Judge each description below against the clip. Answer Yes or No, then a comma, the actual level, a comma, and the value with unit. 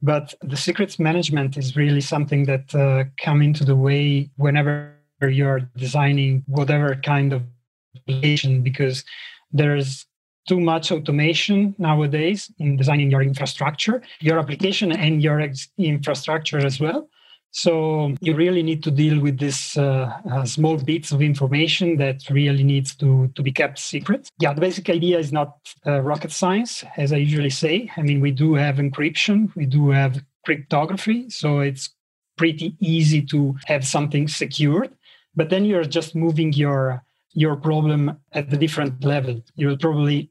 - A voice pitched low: No, medium, 150 Hz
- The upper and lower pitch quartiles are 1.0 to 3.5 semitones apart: Yes, narrow, 2.5 semitones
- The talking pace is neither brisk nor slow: Yes, average, 160 wpm